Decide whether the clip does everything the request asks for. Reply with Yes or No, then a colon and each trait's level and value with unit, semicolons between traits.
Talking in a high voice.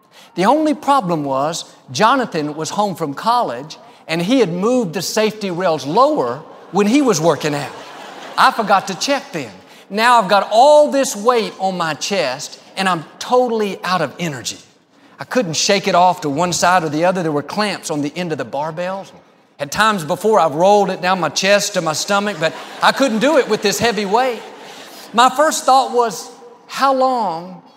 Yes: high, 200 Hz